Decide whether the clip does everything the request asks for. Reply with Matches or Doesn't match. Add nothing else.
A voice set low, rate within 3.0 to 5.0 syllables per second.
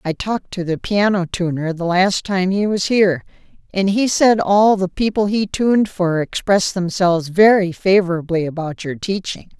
Doesn't match